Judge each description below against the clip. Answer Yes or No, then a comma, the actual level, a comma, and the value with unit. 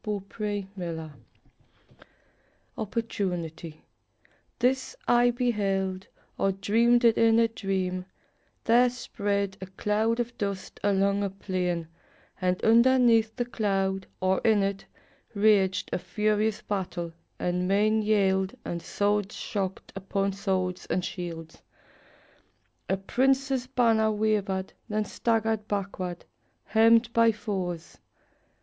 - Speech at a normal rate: No, slow, 110 wpm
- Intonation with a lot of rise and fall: No, average, 3.0 semitones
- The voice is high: Yes, high, 200 Hz